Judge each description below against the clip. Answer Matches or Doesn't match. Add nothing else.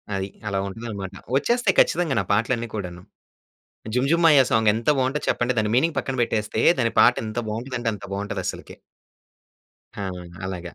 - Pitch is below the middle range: Matches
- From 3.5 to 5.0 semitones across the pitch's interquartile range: Matches